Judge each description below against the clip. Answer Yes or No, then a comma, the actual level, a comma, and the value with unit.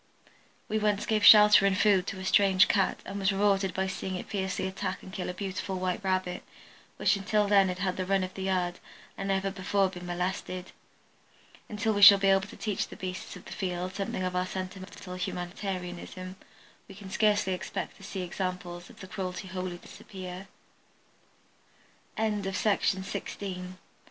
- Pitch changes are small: Yes, narrow, 1.4 semitones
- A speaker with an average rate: Yes, average, 175 wpm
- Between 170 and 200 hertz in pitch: Yes, high, 190 Hz